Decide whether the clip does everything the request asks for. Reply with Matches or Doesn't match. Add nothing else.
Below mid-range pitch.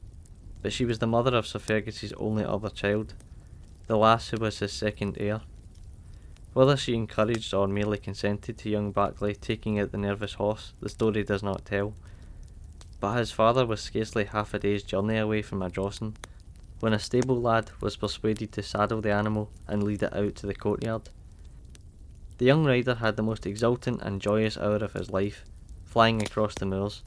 Matches